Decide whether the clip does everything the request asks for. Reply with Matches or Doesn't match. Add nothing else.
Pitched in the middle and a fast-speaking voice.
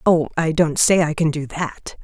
Matches